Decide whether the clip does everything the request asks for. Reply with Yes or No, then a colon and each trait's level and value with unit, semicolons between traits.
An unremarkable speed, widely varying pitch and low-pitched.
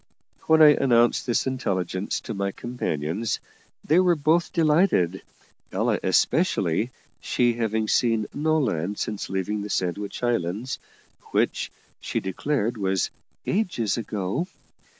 No: slow, 120 wpm; wide, 6.6 semitones; low, 115 Hz